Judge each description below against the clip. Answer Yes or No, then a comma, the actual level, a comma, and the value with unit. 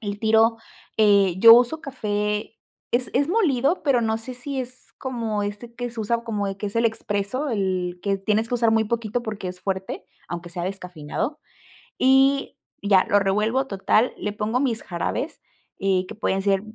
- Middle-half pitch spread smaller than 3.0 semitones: No, average, 3.6 semitones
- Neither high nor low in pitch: No, high, 220 Hz